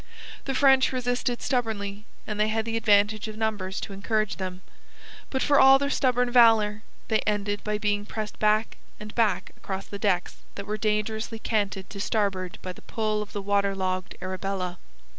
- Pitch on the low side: No, high, 210 Hz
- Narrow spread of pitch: Yes, narrow, 2.1 semitones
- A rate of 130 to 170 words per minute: No, average, 180 wpm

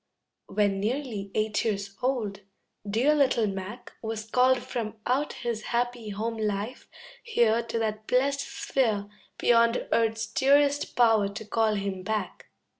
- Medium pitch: No, high, 225 Hz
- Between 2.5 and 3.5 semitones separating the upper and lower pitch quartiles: Yes, average, 2.9 semitones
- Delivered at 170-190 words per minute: No, slow, 135 wpm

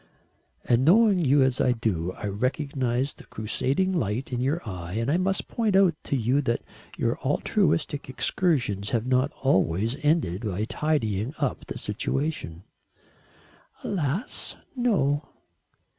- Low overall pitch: Yes, low, 130 Hz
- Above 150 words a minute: No, slow, 135 wpm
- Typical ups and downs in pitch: No, wide, 5.7 semitones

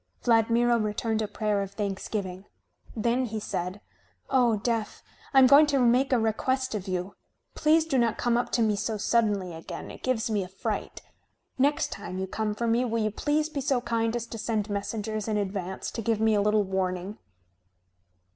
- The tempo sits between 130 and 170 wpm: No, average, 195 wpm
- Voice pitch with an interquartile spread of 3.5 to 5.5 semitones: No, average, 2.9 semitones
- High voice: Yes, high, 220 Hz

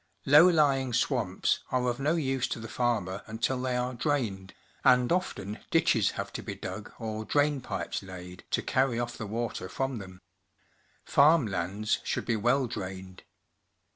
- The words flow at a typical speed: Yes, average, 165 wpm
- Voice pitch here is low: Yes, low, 120 Hz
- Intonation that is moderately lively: Yes, average, 4.6 semitones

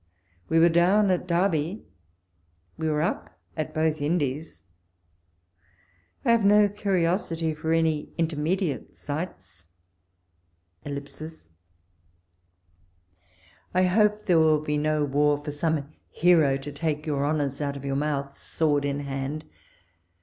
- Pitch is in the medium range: Yes, medium, 150 Hz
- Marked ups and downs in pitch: No, average, 3.1 semitones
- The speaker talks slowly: Yes, slow, 120 wpm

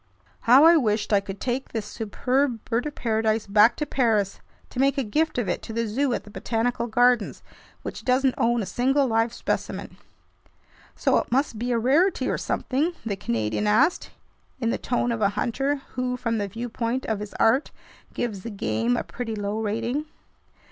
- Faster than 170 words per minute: Yes, average, 190 wpm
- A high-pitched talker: Yes, high, 230 Hz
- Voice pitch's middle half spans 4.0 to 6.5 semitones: No, average, 3.3 semitones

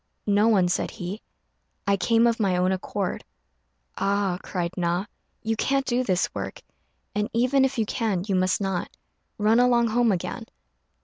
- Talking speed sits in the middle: Yes, average, 165 wpm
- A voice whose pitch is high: Yes, high, 205 Hz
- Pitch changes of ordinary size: Yes, average, 3.9 semitones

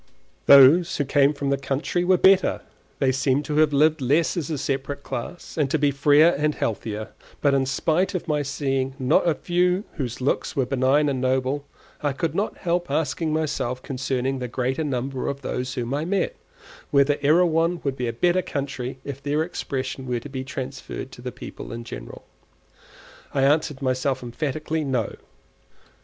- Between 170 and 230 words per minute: Yes, average, 180 wpm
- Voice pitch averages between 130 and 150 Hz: Yes, medium, 140 Hz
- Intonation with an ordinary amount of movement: Yes, average, 3.0 semitones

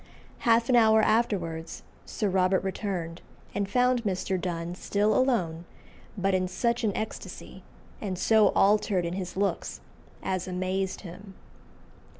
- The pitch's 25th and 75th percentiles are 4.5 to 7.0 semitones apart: No, average, 3.1 semitones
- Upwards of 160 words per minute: No, slow, 135 wpm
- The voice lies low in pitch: No, high, 195 Hz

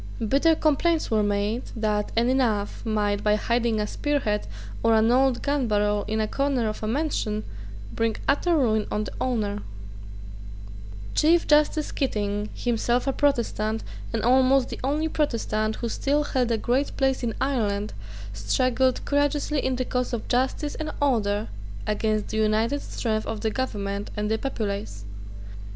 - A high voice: Yes, high, 230 Hz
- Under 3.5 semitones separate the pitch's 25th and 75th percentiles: No, average, 4.1 semitones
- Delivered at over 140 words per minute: Yes, average, 160 wpm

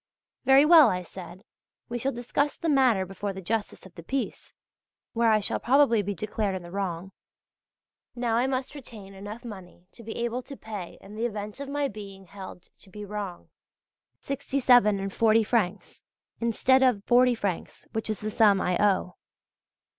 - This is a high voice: Yes, high, 215 Hz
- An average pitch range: Yes, average, 4.0 semitones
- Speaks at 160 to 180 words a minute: Yes, average, 170 wpm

